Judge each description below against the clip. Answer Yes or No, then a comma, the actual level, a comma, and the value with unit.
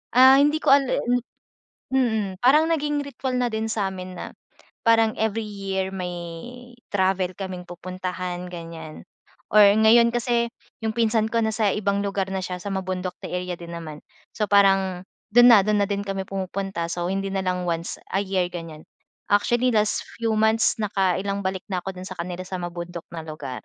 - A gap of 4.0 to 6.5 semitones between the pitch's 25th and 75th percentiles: No, average, 3.4 semitones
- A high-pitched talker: Yes, high, 195 Hz